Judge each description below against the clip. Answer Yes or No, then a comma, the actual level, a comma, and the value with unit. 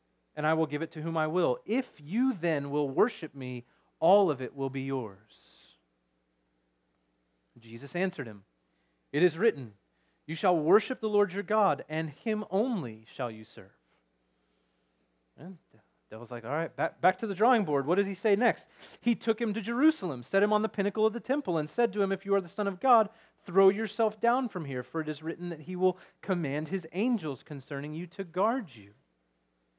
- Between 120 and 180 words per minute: No, fast, 205 wpm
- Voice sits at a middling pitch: Yes, medium, 160 Hz